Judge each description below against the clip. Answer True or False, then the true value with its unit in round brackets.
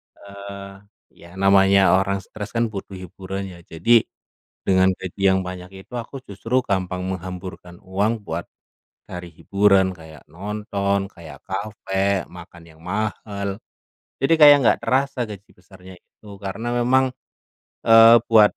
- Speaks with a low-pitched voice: True (100 Hz)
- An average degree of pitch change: False (2.1 semitones)